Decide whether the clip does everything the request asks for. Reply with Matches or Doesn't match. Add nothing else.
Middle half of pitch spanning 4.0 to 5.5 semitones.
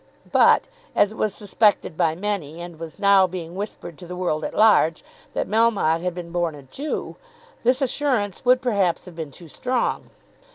Matches